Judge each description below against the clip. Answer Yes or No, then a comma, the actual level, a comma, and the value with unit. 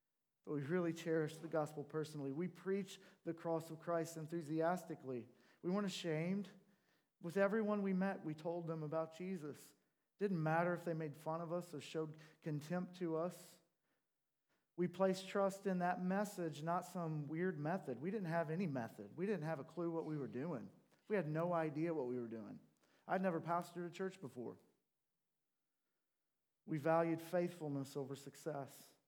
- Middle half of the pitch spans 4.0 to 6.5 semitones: No, average, 2.7 semitones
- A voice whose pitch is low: No, medium, 165 Hz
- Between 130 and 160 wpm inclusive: No, average, 170 wpm